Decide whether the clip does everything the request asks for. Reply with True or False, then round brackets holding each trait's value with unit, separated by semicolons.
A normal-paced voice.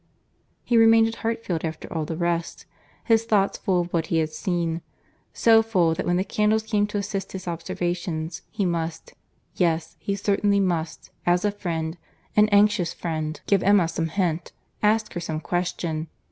True (160 wpm)